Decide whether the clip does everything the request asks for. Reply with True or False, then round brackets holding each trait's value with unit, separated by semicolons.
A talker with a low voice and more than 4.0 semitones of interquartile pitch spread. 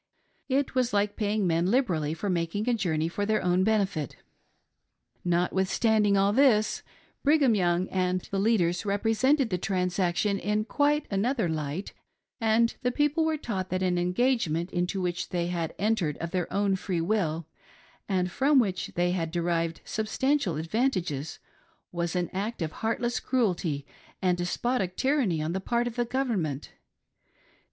False (195 Hz; 4.7 semitones)